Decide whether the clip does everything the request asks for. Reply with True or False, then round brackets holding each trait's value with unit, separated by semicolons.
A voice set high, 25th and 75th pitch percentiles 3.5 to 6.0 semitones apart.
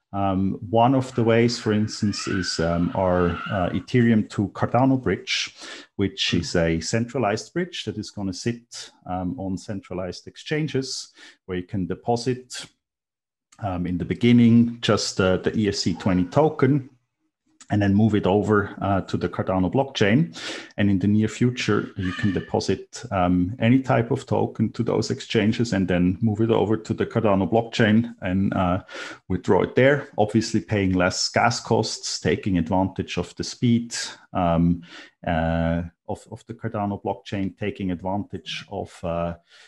False (105 Hz; 4.1 semitones)